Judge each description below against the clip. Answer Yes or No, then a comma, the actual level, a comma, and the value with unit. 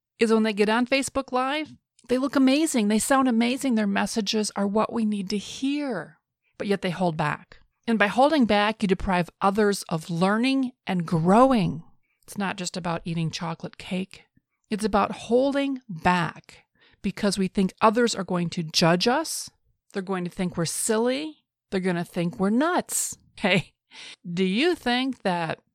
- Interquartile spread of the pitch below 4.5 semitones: No, average, 5.3 semitones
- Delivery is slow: No, average, 170 wpm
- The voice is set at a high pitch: Yes, high, 205 Hz